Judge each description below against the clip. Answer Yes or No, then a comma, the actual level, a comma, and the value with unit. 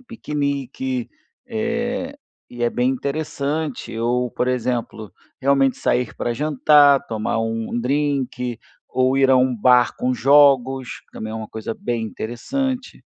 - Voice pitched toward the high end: No, low, 130 Hz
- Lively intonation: No, average, 3.6 semitones